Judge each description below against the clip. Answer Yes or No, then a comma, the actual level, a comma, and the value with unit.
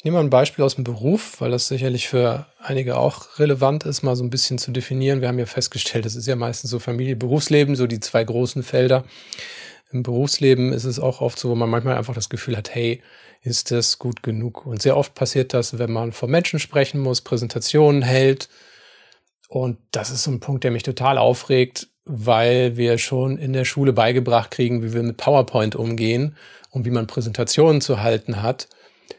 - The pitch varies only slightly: Yes, narrow, 2.1 semitones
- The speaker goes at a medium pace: No, fast, 205 wpm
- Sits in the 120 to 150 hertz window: Yes, low, 125 Hz